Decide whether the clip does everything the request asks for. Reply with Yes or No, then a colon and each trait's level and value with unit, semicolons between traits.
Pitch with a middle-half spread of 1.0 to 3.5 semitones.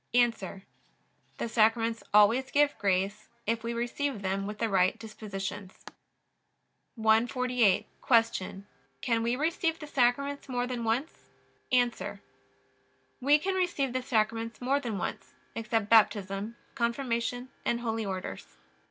Yes: average, 2.9 semitones